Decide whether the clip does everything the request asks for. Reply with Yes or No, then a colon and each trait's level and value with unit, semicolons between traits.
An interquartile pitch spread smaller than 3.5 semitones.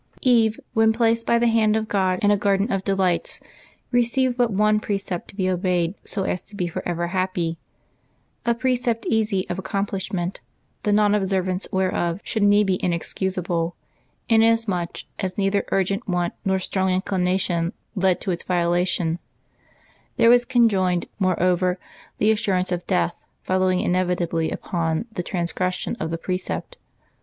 Yes: average, 3.0 semitones